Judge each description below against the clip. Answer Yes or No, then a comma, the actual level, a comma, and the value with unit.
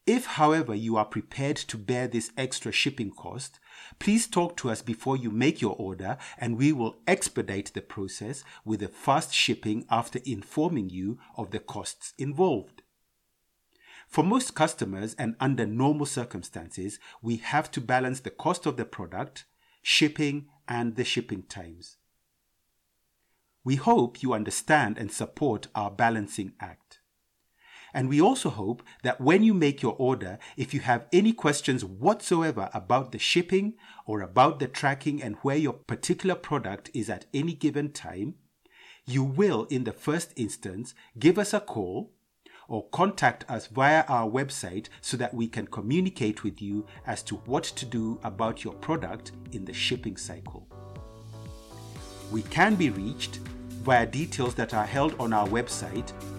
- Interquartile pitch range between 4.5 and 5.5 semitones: Yes, average, 5.1 semitones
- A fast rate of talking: No, average, 155 wpm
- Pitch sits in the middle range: No, low, 120 Hz